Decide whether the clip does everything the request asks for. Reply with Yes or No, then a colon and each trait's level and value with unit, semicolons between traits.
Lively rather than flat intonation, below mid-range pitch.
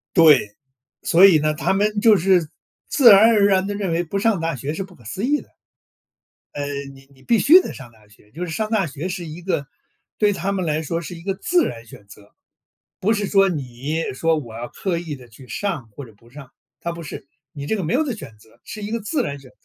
No: wide, 6.4 semitones; medium, 170 Hz